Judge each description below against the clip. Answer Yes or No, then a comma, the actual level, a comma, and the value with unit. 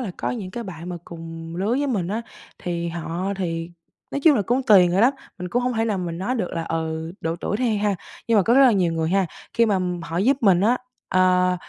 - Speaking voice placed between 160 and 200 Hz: Yes, medium, 185 Hz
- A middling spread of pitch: Yes, average, 5.0 semitones